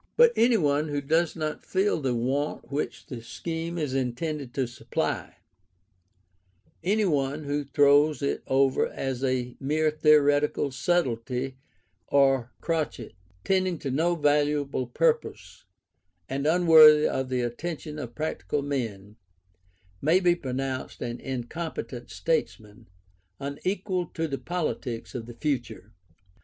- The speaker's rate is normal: No, slow, 125 wpm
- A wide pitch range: No, average, 3.7 semitones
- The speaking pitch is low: No, medium, 145 Hz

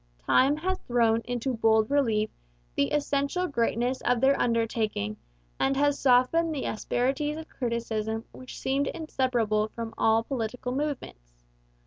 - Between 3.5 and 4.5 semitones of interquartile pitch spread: Yes, average, 3.8 semitones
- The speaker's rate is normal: No, slow, 130 wpm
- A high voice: Yes, high, 245 Hz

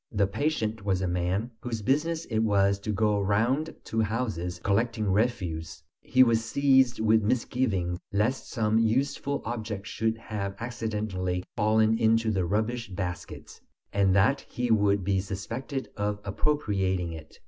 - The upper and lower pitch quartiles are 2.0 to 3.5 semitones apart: Yes, average, 3.1 semitones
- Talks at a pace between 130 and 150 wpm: Yes, average, 145 wpm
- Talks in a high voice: No, low, 110 Hz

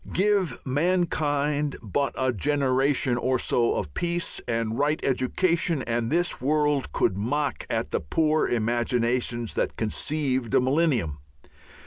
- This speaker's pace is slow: Yes, slow, 125 wpm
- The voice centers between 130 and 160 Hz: Yes, low, 135 Hz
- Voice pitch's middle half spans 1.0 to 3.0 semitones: No, average, 4.2 semitones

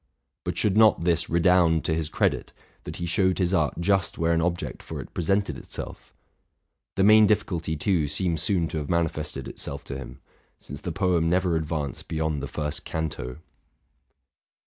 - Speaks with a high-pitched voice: No, very low, 85 Hz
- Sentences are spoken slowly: No, average, 175 wpm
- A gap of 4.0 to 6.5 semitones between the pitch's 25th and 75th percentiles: No, average, 2.8 semitones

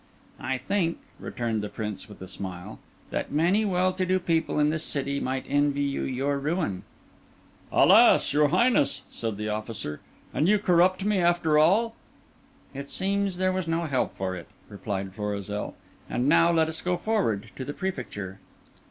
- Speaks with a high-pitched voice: No, medium, 145 Hz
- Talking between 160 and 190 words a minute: Yes, average, 170 wpm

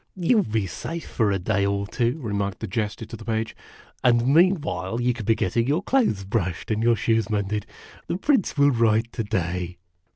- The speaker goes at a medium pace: No, fast, 220 wpm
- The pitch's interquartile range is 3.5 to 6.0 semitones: Yes, average, 3.8 semitones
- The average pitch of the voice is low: Yes, low, 115 Hz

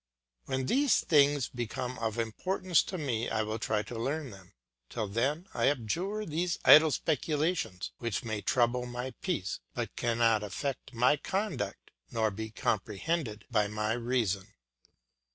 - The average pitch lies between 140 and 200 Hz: No, low, 120 Hz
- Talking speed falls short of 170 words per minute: Yes, average, 145 wpm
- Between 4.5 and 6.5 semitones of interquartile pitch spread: Yes, wide, 5.4 semitones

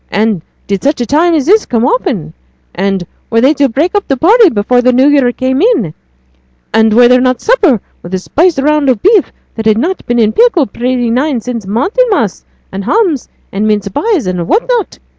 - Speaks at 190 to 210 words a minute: Yes, average, 200 wpm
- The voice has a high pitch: Yes, very high, 255 Hz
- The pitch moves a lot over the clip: Yes, wide, 7.0 semitones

